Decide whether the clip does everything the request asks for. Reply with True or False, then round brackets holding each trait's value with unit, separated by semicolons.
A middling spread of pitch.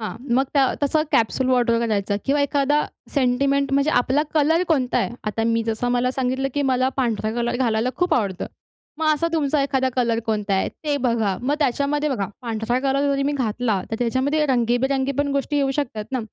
True (3.4 semitones)